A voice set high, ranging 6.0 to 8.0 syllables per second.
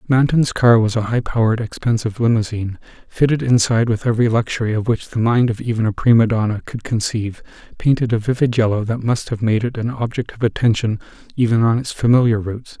No: low, 115 Hz; 6.3 syllables/s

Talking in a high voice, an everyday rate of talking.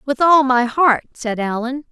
Yes: very high, 260 Hz; average, 190 wpm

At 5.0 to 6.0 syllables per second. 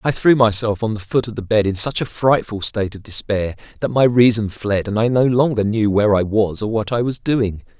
Yes: 5.5 syllables/s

